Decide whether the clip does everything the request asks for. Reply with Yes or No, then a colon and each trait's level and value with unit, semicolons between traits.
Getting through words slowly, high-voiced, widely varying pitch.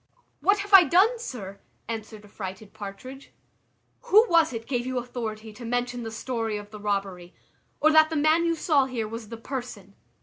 No: average, 180 wpm; high, 240 Hz; wide, 6.4 semitones